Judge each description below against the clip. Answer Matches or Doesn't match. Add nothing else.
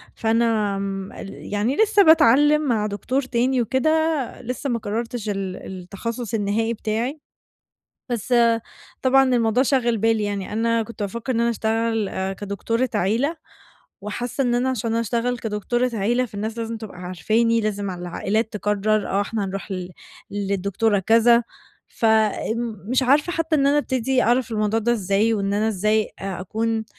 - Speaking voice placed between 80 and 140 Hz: Doesn't match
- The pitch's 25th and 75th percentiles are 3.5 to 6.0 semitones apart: Doesn't match